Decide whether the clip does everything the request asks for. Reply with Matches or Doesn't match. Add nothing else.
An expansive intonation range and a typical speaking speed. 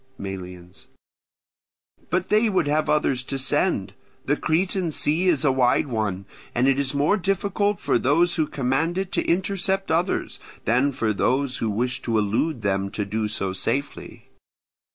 Matches